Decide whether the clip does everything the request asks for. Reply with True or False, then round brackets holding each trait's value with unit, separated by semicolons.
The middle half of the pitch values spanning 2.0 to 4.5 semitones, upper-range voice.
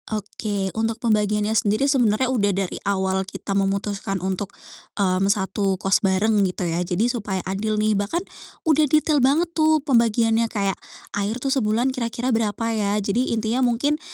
True (3.5 semitones; 215 Hz)